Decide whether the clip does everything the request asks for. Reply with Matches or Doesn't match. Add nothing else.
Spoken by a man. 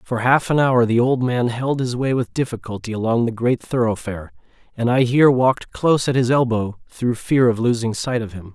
Matches